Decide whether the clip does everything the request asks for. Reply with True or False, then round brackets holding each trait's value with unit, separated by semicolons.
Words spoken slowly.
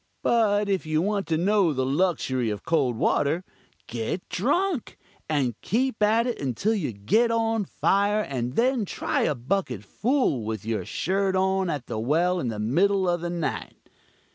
False (170 wpm)